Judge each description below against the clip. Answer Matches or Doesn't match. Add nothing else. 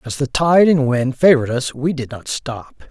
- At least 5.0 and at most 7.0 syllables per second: Doesn't match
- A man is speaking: Matches